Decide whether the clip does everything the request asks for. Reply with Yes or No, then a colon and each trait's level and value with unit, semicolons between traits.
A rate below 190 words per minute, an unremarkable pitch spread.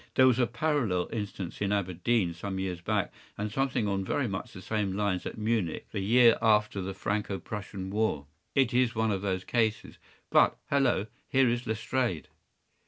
Yes: average, 170 wpm; average, 3.7 semitones